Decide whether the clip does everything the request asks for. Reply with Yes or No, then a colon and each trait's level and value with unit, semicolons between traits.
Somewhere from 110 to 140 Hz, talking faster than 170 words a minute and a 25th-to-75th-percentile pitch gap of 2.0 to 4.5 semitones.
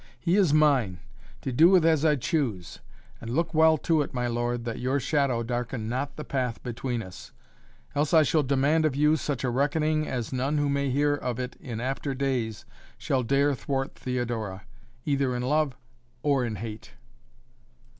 Yes: low, 135 Hz; average, 180 wpm; average, 3.5 semitones